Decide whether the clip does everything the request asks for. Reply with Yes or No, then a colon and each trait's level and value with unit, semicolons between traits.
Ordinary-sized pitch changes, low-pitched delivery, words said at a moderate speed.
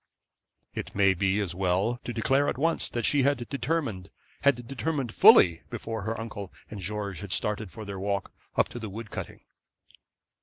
Yes: average, 3.9 semitones; low, 110 Hz; average, 180 wpm